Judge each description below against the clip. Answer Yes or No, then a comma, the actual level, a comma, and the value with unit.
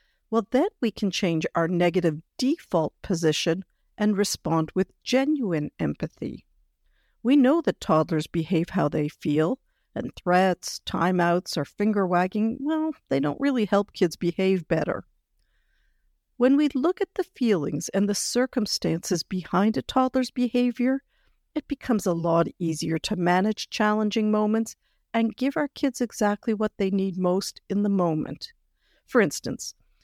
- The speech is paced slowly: No, average, 145 wpm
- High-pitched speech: Yes, high, 200 Hz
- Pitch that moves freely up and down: Yes, wide, 6.1 semitones